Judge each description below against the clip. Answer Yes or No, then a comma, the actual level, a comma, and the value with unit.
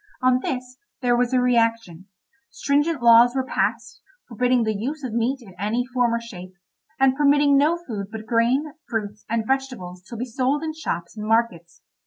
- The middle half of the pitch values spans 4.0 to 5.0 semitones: No, average, 3.2 semitones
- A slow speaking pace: No, average, 180 wpm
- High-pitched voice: Yes, high, 240 Hz